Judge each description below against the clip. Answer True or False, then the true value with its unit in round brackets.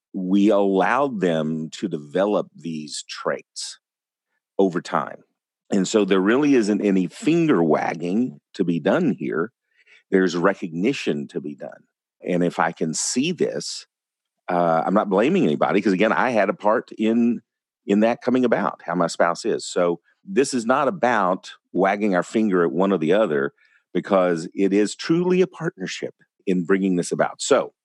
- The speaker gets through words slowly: False (165 wpm)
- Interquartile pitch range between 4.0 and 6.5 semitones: False (3.5 semitones)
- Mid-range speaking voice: False (95 Hz)